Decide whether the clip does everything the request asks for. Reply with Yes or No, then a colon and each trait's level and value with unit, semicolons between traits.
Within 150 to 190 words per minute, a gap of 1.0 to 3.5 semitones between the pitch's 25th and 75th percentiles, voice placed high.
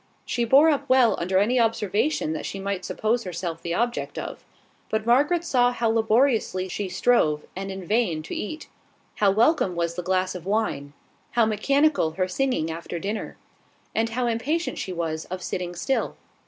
No: average, 175 wpm; average, 5.3 semitones; high, 210 Hz